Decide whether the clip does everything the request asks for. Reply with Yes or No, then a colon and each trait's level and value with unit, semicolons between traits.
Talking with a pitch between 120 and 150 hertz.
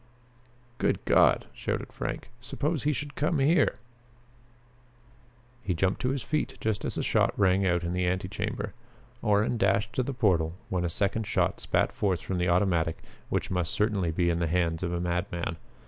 No: very low, 95 Hz